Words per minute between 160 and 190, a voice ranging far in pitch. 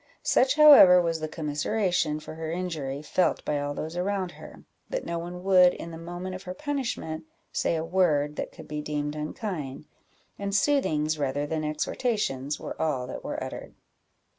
No: average, 175 wpm; average, 3.7 semitones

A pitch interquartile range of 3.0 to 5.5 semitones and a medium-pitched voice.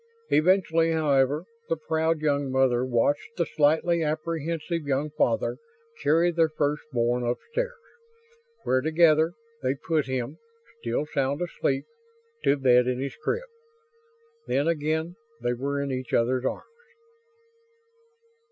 Yes: average, 3.6 semitones; medium, 150 Hz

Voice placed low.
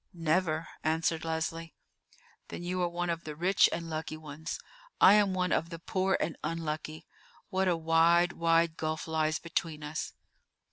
No: medium, 165 Hz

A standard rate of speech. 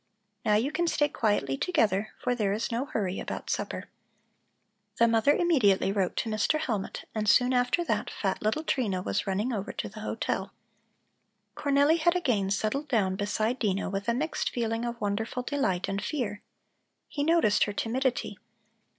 Yes: average, 170 wpm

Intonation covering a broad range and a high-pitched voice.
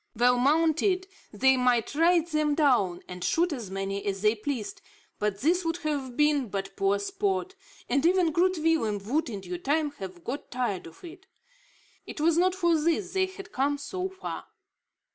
Yes: wide, 8.3 semitones; very high, 290 Hz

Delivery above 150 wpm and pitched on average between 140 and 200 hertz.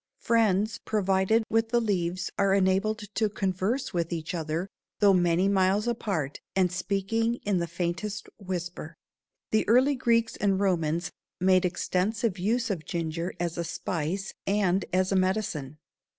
No: average, 145 wpm; high, 190 Hz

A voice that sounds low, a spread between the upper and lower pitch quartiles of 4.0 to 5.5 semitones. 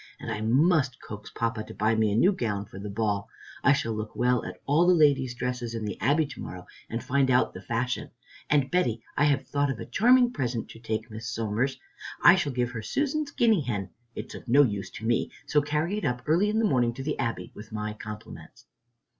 Yes: low, 125 Hz; average, 5.0 semitones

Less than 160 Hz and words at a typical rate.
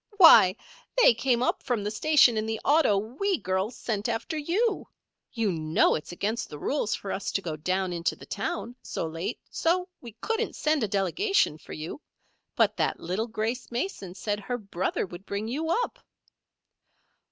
No: high, 220 Hz; average, 175 wpm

